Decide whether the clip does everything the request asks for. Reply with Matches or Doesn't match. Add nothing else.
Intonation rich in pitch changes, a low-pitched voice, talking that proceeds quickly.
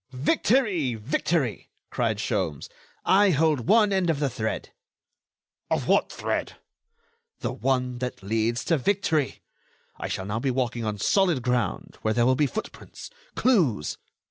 Doesn't match